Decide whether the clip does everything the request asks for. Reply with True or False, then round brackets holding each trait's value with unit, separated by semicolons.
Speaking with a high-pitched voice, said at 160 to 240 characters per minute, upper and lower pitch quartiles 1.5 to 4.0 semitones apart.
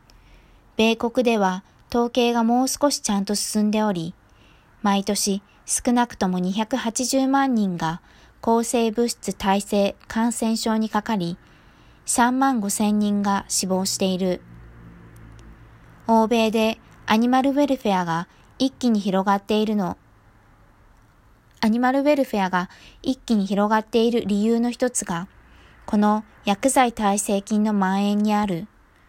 True (210 Hz; 235 characters per minute; 3.6 semitones)